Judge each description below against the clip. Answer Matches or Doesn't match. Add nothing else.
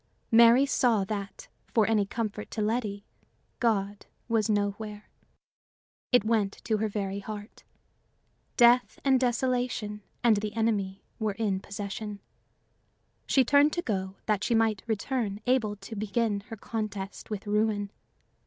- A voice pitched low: Doesn't match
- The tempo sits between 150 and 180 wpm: Doesn't match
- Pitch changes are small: Matches